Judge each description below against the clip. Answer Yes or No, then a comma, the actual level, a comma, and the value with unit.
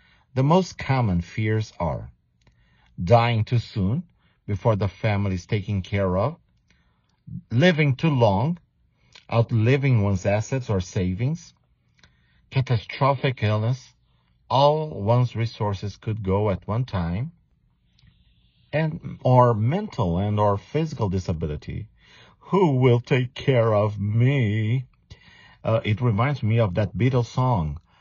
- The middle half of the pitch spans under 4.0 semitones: No, average, 4.9 semitones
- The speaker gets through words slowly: Yes, slow, 115 wpm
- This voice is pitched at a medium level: No, low, 115 Hz